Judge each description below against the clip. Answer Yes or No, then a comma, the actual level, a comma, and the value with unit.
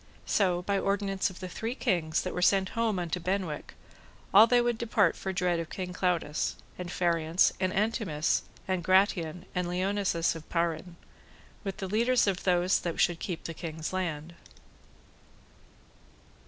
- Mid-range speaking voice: Yes, medium, 180 Hz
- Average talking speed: Yes, average, 155 wpm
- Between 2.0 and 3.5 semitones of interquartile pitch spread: Yes, narrow, 2.5 semitones